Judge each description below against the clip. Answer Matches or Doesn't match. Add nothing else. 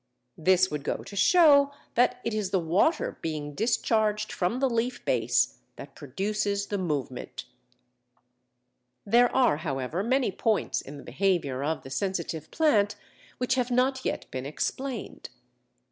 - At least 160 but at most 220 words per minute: Doesn't match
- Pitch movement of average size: Doesn't match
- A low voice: Doesn't match